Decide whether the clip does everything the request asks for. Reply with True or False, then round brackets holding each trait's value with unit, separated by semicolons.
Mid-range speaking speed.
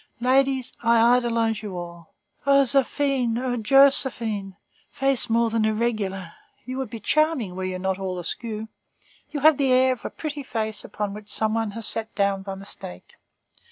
True (170 wpm)